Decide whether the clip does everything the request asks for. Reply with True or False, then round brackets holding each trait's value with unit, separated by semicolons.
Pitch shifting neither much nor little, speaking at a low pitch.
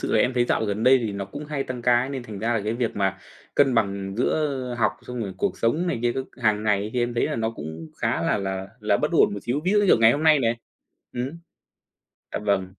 True (4.0 semitones; 115 Hz)